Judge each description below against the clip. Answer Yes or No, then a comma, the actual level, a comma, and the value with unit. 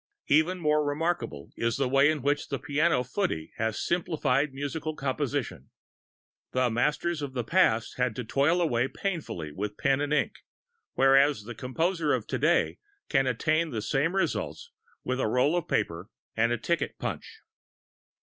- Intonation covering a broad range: No, average, 4.3 semitones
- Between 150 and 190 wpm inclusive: Yes, average, 155 wpm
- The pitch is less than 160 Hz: Yes, medium, 140 Hz